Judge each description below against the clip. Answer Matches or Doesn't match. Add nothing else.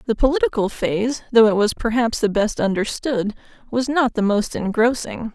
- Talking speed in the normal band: Matches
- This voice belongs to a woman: Matches